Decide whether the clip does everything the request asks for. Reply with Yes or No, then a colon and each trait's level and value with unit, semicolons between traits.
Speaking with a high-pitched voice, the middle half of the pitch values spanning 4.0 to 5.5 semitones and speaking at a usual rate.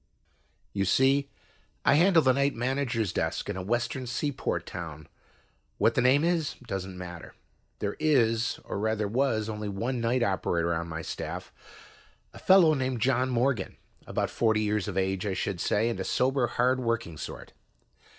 No: low, 115 Hz; average, 5.1 semitones; average, 165 wpm